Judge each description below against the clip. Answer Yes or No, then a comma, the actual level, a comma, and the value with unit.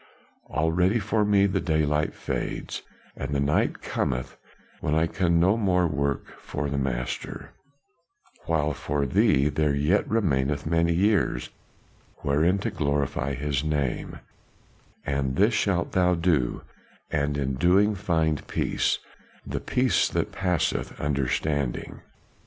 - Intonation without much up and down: No, average, 4.3 semitones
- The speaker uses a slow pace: Yes, slow, 130 wpm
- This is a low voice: Yes, very low, 75 Hz